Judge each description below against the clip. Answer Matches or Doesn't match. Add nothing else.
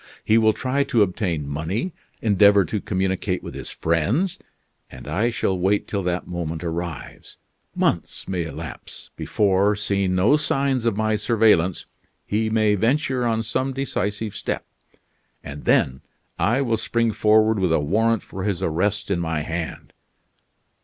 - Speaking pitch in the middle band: Doesn't match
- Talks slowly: Doesn't match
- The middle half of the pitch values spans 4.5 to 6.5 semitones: Doesn't match